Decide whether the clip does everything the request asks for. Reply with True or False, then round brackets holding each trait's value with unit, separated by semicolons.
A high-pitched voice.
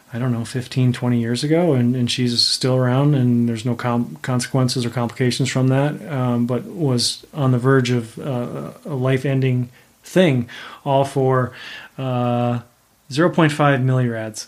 False (125 Hz)